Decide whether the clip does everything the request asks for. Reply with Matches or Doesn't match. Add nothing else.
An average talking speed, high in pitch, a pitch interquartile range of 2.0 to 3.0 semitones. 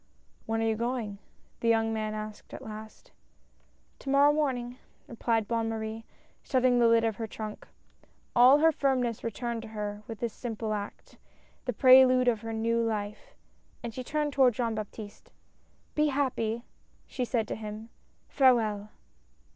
Matches